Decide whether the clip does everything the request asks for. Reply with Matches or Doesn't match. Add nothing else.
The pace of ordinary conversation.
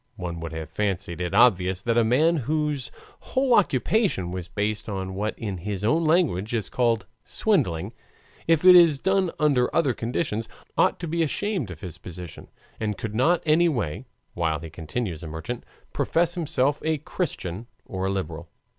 Matches